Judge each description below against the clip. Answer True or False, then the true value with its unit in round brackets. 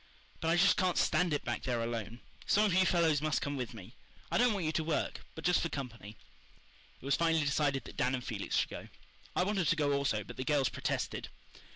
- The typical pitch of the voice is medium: True (145 Hz)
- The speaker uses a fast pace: True (235 wpm)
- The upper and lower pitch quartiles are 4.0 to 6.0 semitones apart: True (5.1 semitones)